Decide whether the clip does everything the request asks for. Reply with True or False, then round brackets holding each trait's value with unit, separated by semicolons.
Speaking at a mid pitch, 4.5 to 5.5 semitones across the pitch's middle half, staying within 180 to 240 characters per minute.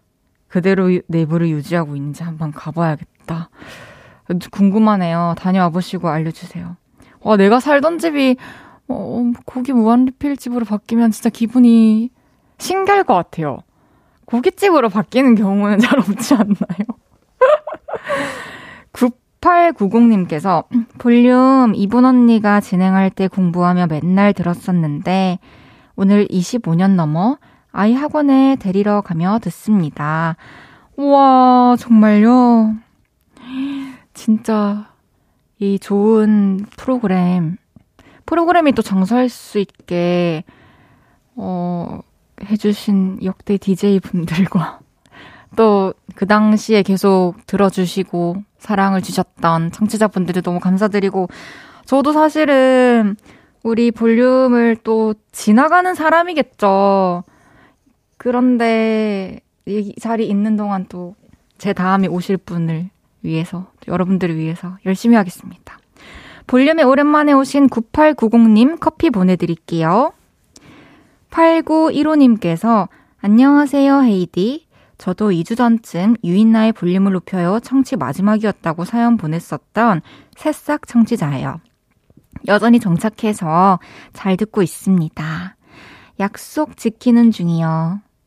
False (210 Hz; 5.1 semitones; 235 characters per minute)